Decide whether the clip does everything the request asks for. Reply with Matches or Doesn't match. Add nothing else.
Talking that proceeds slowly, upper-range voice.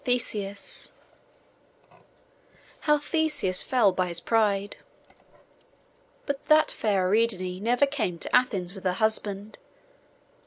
Matches